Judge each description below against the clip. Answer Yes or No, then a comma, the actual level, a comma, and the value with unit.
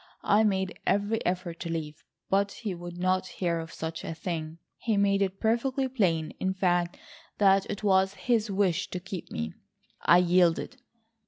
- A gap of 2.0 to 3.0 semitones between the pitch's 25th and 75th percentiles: Yes, average, 2.7 semitones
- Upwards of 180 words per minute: No, average, 170 wpm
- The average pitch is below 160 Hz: No, high, 190 Hz